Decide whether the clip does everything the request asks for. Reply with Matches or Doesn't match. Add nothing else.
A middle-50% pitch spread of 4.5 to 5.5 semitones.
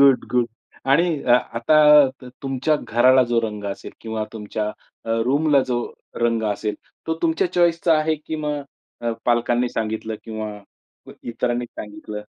Matches